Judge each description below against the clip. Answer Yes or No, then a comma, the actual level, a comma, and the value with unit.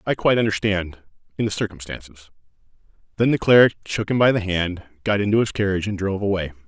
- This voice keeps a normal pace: Yes, average, 180 wpm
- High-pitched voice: No, low, 100 Hz